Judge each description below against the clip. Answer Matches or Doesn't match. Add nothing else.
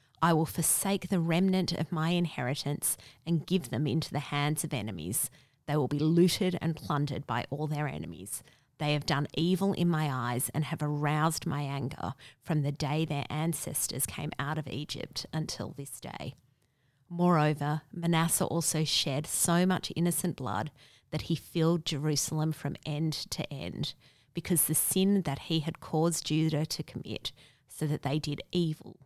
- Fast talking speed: Doesn't match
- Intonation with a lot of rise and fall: Doesn't match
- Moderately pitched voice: Matches